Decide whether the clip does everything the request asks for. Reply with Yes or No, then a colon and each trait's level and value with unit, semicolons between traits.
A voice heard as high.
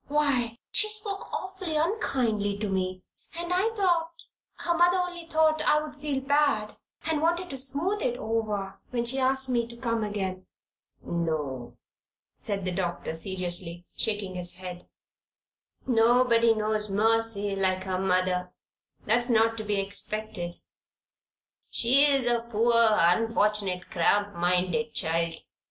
Yes: high, 225 Hz